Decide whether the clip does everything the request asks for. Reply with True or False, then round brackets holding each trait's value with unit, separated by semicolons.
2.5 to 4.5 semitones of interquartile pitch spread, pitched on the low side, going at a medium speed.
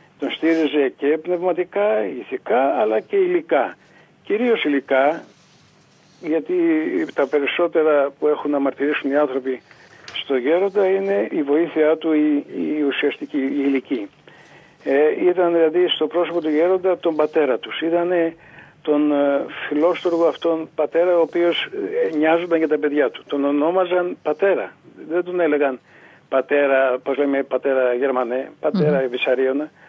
False (3.8 semitones; 155 Hz; 125 wpm)